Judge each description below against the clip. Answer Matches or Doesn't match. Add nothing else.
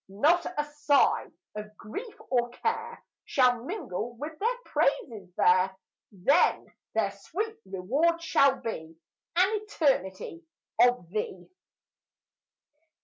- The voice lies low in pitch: Doesn't match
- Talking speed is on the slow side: Matches